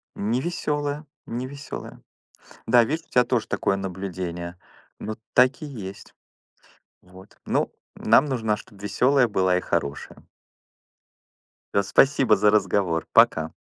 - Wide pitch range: Yes, wide, 5.7 semitones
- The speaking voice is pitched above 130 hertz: No, low, 110 Hz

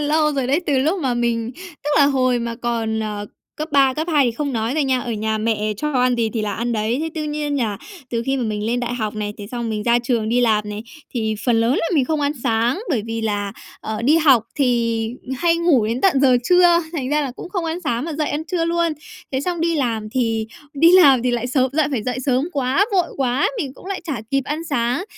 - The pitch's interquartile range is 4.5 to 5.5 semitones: Yes, average, 4.8 semitones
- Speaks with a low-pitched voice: No, very high, 255 Hz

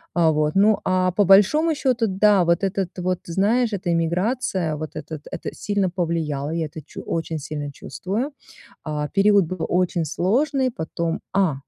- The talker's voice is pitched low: No, medium, 185 Hz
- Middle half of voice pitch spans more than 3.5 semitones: Yes, average, 4.0 semitones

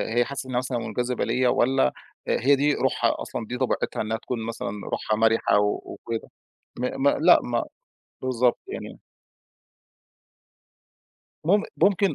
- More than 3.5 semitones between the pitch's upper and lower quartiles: No, average, 2.8 semitones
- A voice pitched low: Yes, low, 125 Hz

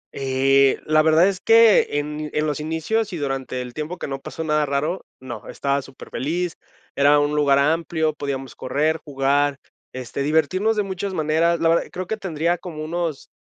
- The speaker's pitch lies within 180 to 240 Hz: No, medium, 155 Hz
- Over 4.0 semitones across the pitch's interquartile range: No, average, 3.4 semitones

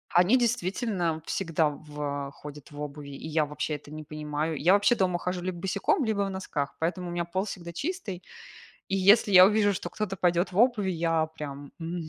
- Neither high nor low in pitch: Yes, medium, 175 Hz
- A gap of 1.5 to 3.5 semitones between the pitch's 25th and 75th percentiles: No, average, 4.2 semitones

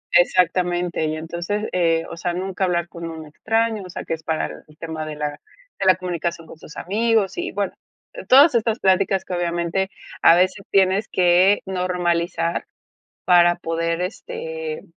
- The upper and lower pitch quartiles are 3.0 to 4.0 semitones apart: No, narrow, 2.6 semitones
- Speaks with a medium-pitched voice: Yes, medium, 180 Hz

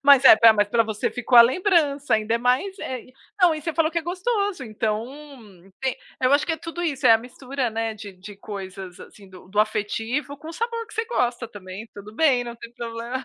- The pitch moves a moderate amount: No, wide, 6.2 semitones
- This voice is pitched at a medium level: No, high, 245 Hz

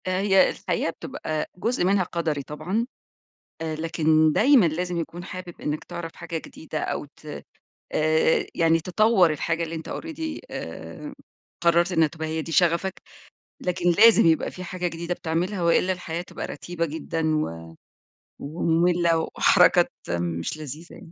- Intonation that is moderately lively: No, narrow, 2.3 semitones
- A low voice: No, medium, 165 Hz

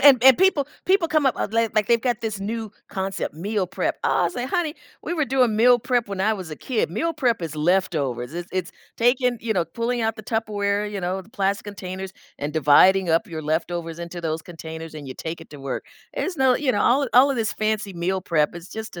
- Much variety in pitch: Yes, wide, 5.9 semitones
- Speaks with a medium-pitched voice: No, high, 200 Hz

